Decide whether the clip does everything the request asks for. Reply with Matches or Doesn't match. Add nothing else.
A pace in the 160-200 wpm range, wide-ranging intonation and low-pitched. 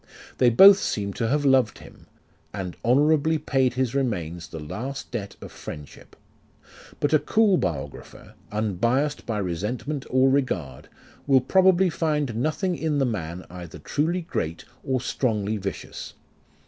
Doesn't match